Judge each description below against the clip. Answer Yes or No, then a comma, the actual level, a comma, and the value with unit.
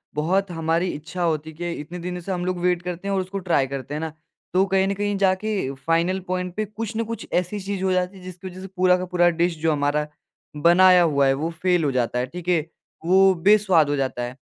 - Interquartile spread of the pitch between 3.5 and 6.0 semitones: No, average, 3.0 semitones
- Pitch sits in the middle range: Yes, medium, 180 Hz